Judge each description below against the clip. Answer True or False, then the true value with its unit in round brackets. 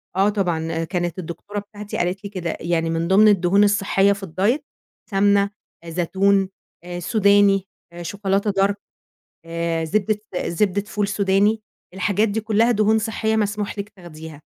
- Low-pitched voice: False (195 Hz)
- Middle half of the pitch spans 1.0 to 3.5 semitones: True (2.9 semitones)